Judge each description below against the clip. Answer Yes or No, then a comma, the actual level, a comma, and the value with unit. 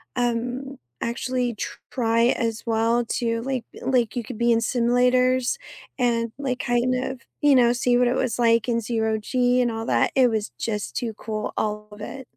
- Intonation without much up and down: Yes, narrow, 1.7 semitones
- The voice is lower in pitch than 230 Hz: No, high, 240 Hz